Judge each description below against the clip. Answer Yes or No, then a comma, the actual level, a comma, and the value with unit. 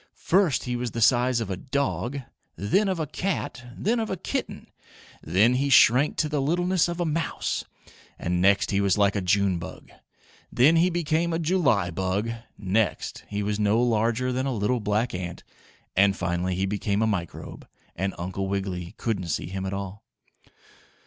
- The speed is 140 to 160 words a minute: No, average, 180 wpm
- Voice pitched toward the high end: No, low, 110 Hz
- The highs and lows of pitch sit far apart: Yes, wide, 6.4 semitones